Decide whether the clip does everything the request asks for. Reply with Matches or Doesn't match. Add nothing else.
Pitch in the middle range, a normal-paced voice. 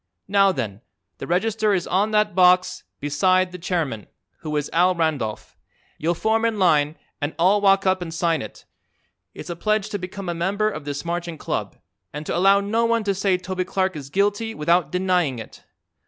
Matches